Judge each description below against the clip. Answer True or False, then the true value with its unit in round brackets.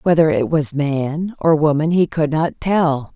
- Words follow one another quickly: False (190 wpm)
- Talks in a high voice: False (155 Hz)